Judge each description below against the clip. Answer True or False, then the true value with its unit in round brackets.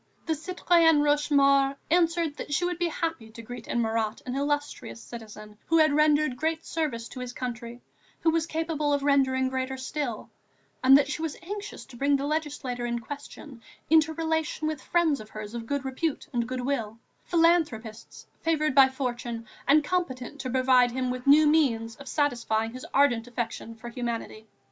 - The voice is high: True (275 Hz)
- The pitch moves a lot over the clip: False (4.4 semitones)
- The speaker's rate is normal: True (175 wpm)